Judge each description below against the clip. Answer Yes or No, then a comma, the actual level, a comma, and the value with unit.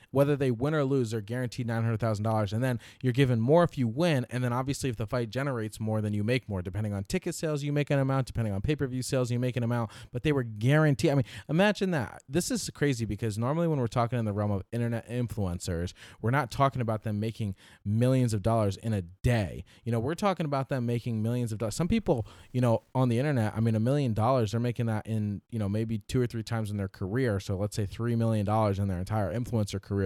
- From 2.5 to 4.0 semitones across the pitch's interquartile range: Yes, average, 3.6 semitones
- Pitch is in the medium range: No, low, 120 Hz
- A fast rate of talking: Yes, fast, 250 wpm